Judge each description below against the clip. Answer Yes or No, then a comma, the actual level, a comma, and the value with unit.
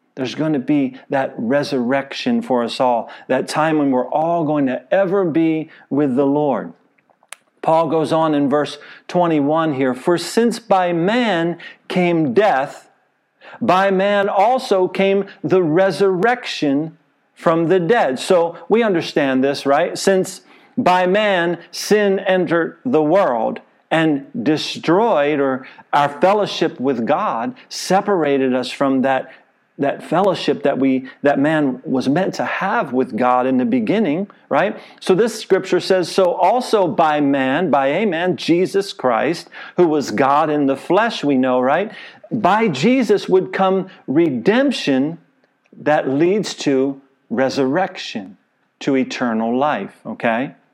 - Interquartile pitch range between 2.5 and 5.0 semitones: No, wide, 5.5 semitones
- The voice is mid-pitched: Yes, medium, 165 Hz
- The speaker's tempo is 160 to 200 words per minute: No, average, 140 wpm